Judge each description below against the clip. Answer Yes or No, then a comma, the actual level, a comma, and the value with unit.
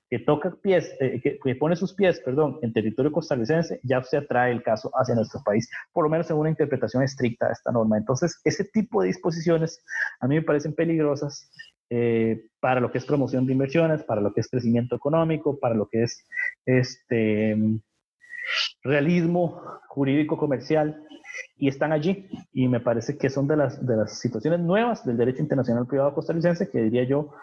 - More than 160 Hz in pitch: No, medium, 140 Hz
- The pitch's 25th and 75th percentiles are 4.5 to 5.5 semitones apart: Yes, average, 5.1 semitones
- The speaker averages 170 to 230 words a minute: Yes, average, 185 wpm